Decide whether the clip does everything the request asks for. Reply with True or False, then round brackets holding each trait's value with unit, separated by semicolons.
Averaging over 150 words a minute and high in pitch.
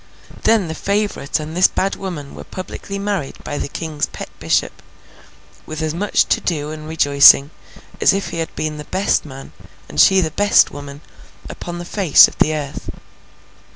False (180 wpm; 160 Hz)